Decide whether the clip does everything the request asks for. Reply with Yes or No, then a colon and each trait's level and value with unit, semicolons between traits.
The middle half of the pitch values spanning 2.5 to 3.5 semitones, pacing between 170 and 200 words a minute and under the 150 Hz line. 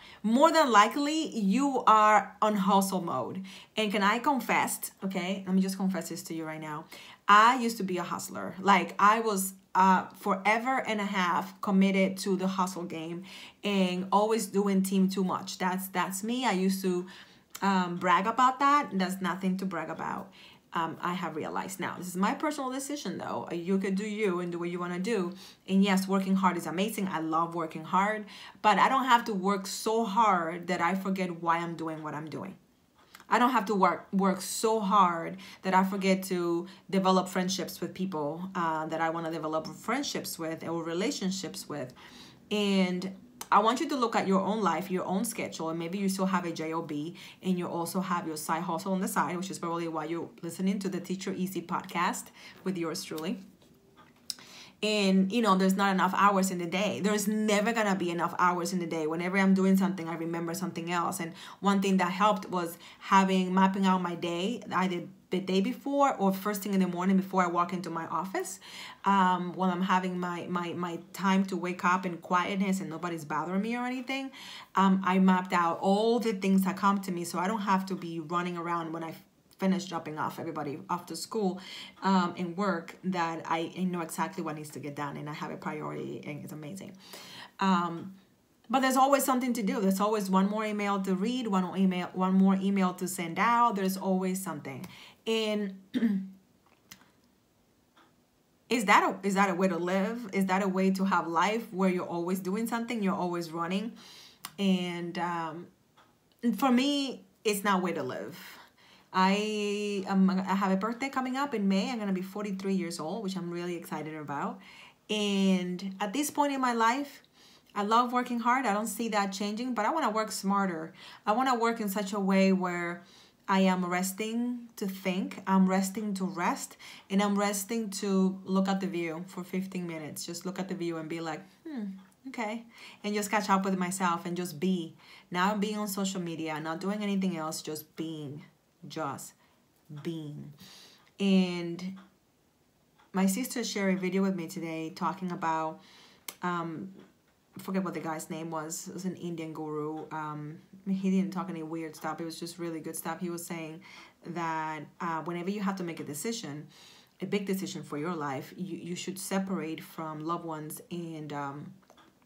No: average, 3.0 semitones; average, 195 wpm; high, 190 Hz